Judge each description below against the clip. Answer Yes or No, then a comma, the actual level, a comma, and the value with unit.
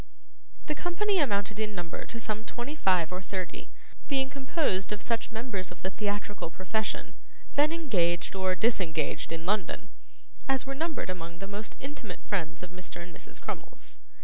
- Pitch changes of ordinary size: No, wide, 6.2 semitones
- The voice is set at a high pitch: Yes, high, 205 Hz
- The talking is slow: No, average, 165 wpm